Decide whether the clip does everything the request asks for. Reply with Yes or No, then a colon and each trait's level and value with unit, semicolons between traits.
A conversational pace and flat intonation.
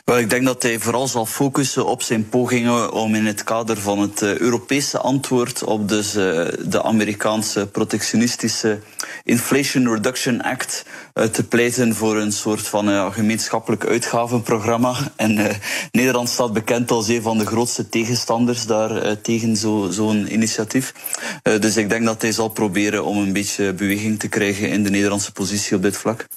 Yes: average, 155 wpm; narrow, 2.2 semitones